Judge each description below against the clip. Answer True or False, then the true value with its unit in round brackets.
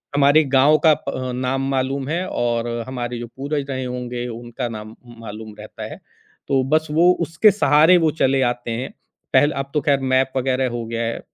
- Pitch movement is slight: False (3.1 semitones)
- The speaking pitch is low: True (130 Hz)